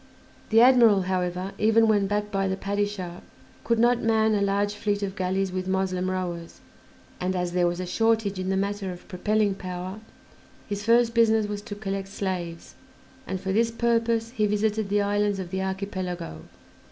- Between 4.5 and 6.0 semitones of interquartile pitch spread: No, narrow, 2.6 semitones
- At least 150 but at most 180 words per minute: Yes, average, 175 wpm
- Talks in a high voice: Yes, high, 200 Hz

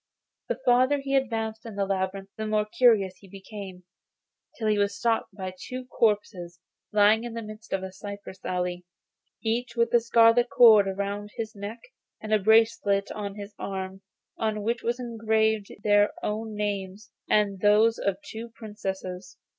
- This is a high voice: Yes, high, 210 Hz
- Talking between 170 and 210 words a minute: No, average, 160 wpm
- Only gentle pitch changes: Yes, narrow, 2.3 semitones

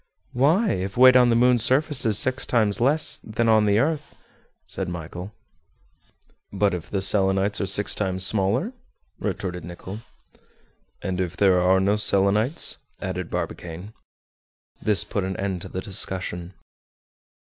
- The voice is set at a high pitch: No, low, 100 Hz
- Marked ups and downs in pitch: No, average, 4.1 semitones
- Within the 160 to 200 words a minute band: No, average, 145 wpm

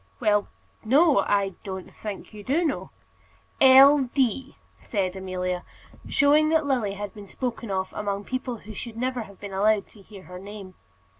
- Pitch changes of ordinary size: Yes, average, 4.8 semitones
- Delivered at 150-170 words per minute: Yes, average, 165 wpm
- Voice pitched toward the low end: No, high, 210 Hz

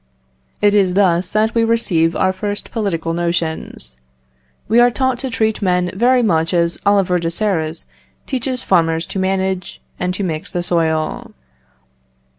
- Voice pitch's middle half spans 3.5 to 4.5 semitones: Yes, average, 4.2 semitones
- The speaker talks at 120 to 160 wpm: Yes, average, 150 wpm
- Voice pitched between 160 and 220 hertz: Yes, medium, 185 Hz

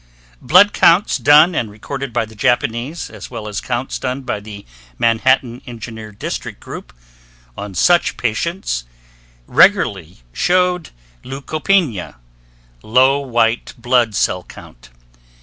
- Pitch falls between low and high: No, low, 120 Hz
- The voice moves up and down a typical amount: Yes, average, 4.6 semitones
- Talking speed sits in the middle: No, slow, 115 wpm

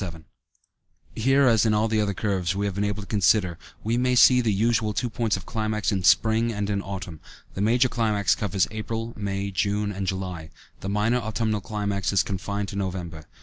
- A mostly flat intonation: Yes, narrow, 2.3 semitones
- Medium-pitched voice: No, low, 105 Hz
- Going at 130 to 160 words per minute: No, average, 200 wpm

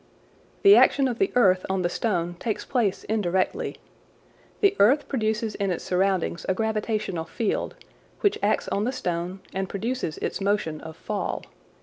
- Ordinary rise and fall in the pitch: Yes, average, 3.8 semitones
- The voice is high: Yes, high, 205 Hz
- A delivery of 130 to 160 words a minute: Yes, average, 155 wpm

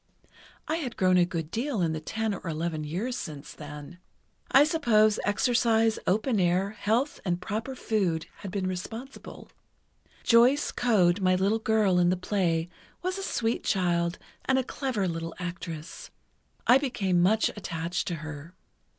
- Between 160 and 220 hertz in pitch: Yes, high, 190 Hz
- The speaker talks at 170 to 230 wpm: No, average, 155 wpm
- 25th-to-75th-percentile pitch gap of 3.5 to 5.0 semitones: Yes, average, 4.7 semitones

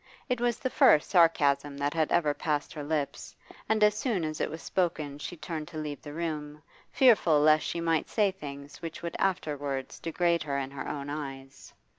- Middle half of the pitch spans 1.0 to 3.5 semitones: Yes, average, 2.9 semitones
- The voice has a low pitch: No, medium, 155 Hz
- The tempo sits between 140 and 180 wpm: No, average, 195 wpm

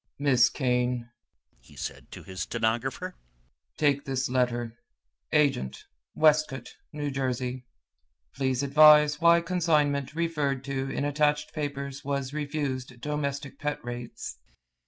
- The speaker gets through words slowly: Yes, slow, 115 wpm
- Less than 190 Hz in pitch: Yes, medium, 140 Hz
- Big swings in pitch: No, average, 2.8 semitones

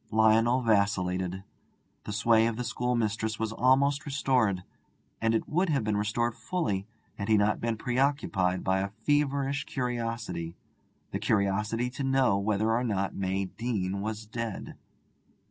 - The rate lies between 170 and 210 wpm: No, average, 145 wpm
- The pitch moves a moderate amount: Yes, average, 3.6 semitones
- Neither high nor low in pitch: No, low, 110 Hz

